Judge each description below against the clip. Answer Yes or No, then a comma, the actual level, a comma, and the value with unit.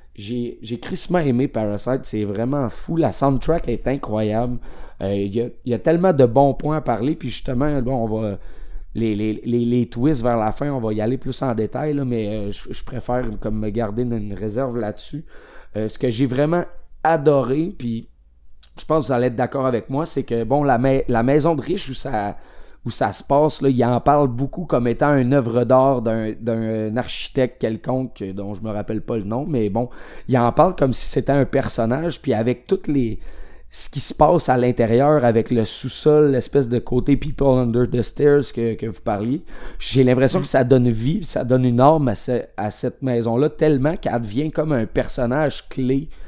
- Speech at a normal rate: Yes, average, 210 wpm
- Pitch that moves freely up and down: No, average, 3.6 semitones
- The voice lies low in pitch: Yes, low, 125 Hz